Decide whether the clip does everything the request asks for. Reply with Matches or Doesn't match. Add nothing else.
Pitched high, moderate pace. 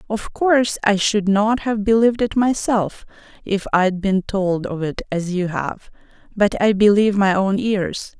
Matches